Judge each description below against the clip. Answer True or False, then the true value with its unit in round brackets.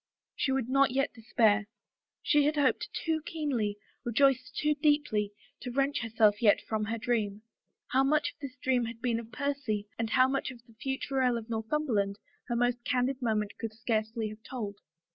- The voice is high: True (245 Hz)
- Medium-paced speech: True (180 wpm)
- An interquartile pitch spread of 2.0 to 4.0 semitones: True (3.7 semitones)